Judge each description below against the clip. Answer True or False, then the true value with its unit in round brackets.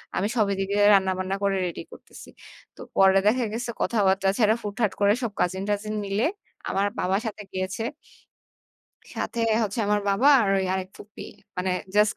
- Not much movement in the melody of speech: True (1.9 semitones)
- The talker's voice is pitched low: False (200 Hz)